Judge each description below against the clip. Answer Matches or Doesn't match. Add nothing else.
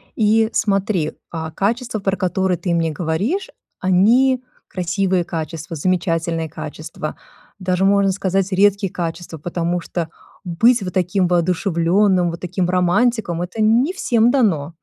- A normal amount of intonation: Matches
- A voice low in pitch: Doesn't match